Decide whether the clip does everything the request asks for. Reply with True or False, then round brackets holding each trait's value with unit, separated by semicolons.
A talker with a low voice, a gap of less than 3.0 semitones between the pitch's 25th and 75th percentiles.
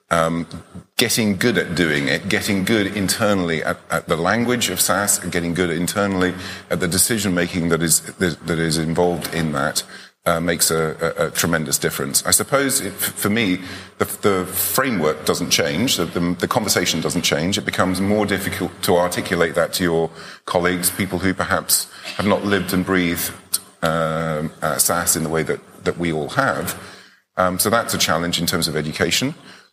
True (90 Hz; 2.6 semitones)